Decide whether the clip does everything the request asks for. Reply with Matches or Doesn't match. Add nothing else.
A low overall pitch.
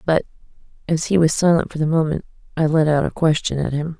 Doesn't match